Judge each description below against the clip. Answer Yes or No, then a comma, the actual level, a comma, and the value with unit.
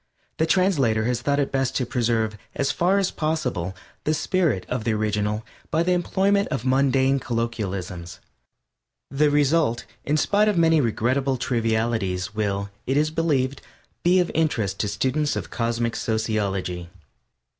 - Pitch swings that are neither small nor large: No, wide, 5.8 semitones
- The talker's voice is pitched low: Yes, low, 125 Hz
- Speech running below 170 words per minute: Yes, average, 145 wpm